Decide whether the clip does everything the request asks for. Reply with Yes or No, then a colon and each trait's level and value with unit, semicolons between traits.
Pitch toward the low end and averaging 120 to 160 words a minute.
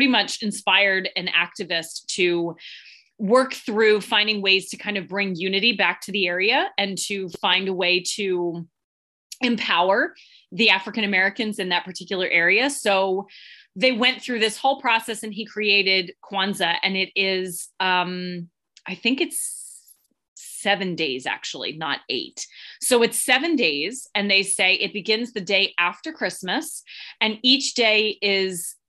No: high, 200 Hz; average, 150 wpm